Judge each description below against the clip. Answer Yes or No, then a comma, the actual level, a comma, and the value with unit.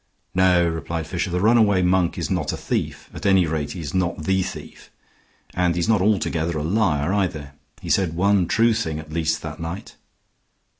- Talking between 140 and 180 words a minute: No, average, 190 wpm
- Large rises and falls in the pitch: No, average, 2.9 semitones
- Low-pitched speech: Yes, very low, 90 Hz